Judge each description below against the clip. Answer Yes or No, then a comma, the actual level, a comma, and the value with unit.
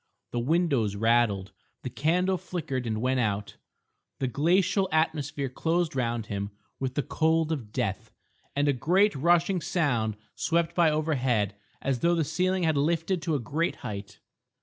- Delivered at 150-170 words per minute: Yes, average, 155 wpm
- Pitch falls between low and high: Yes, medium, 145 Hz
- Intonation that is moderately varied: No, wide, 5.9 semitones